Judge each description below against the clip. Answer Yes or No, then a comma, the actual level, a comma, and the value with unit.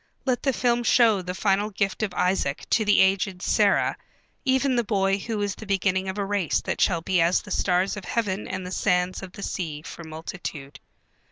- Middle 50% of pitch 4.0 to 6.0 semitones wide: No, narrow, 2.6 semitones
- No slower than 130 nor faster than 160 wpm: No, fast, 205 wpm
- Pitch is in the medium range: No, high, 195 Hz